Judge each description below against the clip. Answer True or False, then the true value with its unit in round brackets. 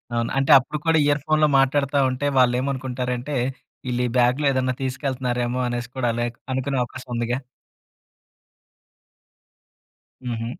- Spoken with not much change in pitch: True (2.0 semitones)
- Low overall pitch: True (130 Hz)